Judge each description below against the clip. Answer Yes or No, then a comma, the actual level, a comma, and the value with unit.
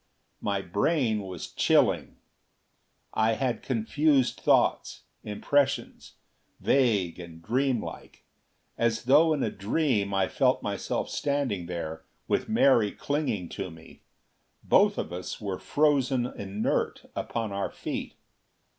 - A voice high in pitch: No, low, 110 Hz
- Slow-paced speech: Yes, slow, 115 wpm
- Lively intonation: Yes, wide, 6.0 semitones